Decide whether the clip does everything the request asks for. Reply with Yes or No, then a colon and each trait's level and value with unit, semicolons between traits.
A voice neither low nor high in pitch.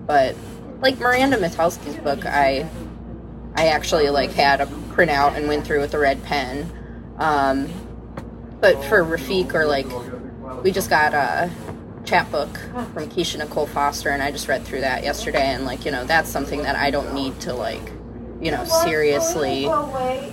Yes: medium, 150 Hz